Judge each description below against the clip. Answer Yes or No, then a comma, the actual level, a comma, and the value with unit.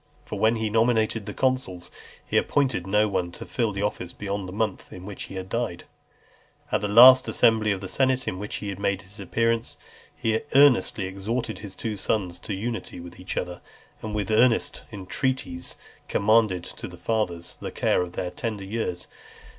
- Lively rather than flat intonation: No, average, 3.4 semitones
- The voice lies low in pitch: Yes, low, 105 Hz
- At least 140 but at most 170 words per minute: No, average, 180 wpm